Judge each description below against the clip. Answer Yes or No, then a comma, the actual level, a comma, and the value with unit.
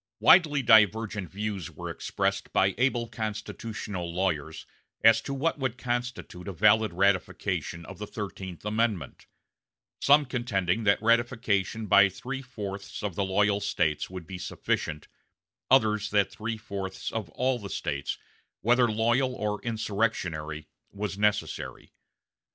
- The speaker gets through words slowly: Yes, slow, 130 wpm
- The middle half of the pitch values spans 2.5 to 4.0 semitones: Yes, average, 3.5 semitones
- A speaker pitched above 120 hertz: No, low, 105 Hz